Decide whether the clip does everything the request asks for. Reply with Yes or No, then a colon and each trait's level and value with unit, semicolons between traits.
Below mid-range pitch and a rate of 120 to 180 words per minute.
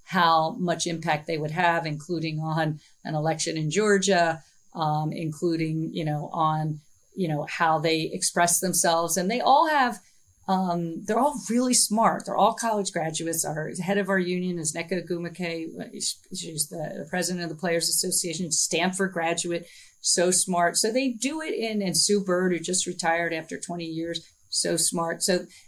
No: medium, 170 Hz; average, 170 wpm